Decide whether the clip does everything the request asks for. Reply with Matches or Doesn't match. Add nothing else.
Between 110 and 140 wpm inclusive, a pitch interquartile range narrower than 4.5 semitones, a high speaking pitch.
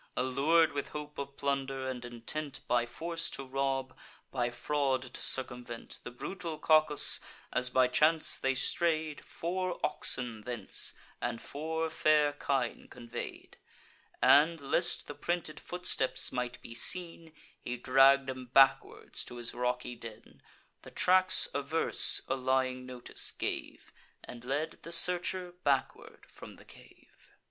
Doesn't match